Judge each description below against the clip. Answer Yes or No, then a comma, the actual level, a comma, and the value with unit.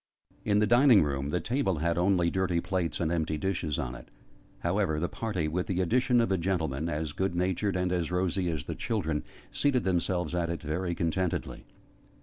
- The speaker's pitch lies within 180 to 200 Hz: No, very low, 90 Hz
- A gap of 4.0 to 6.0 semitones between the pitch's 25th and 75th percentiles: No, average, 3.0 semitones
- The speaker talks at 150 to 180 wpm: No, average, 190 wpm